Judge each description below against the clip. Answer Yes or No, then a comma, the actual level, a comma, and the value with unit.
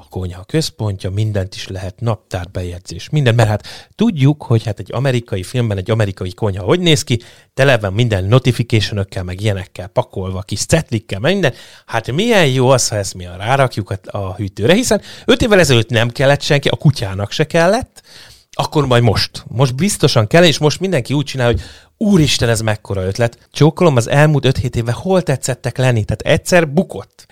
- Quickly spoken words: Yes, fast, 180 wpm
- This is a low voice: Yes, low, 120 Hz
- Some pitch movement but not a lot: No, wide, 6.0 semitones